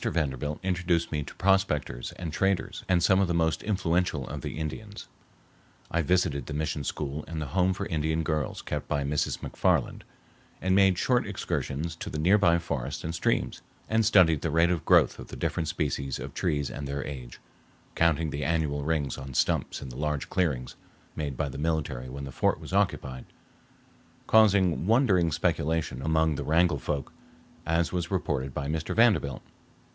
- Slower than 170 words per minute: No, average, 175 wpm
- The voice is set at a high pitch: No, very low, 80 Hz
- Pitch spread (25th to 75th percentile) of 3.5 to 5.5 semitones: Yes, average, 3.8 semitones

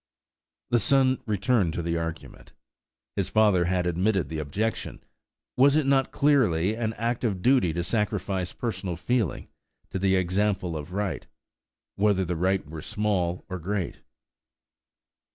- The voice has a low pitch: Yes, very low, 95 Hz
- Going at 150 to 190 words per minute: No, average, 140 wpm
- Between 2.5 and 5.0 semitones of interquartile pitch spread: Yes, average, 4.3 semitones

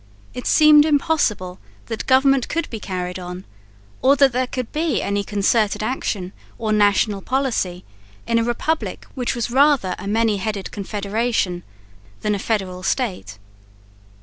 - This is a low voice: No, high, 220 Hz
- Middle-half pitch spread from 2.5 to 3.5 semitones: No, average, 4.9 semitones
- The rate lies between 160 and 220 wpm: No, average, 145 wpm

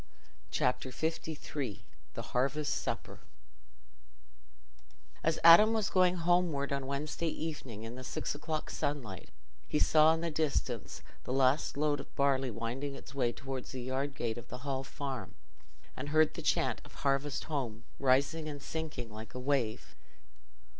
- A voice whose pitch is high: No, medium, 140 Hz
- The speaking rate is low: No, average, 150 wpm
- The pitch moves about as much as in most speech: Yes, average, 3.3 semitones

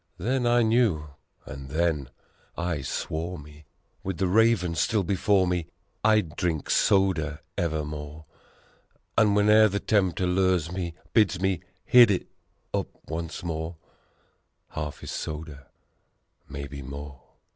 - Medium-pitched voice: No, very low, 85 Hz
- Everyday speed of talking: No, slow, 125 wpm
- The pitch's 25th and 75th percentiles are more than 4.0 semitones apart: Yes, average, 4.4 semitones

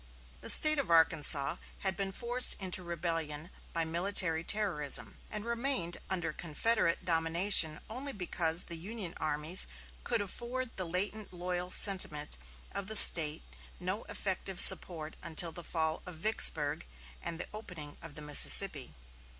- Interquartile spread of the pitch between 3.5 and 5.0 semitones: Yes, average, 3.8 semitones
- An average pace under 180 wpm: Yes, average, 140 wpm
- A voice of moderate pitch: Yes, medium, 175 Hz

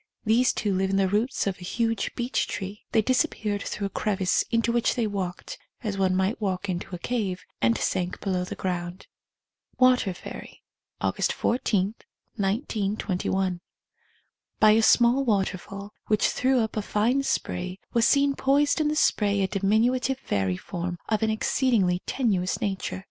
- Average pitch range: Yes, average, 3.8 semitones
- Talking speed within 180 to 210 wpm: No, average, 165 wpm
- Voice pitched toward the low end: No, high, 205 Hz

